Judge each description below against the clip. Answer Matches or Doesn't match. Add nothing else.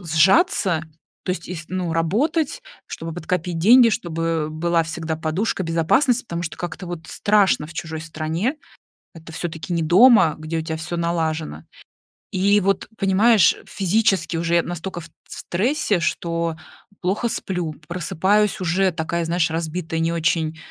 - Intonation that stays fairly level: Doesn't match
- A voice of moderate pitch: Matches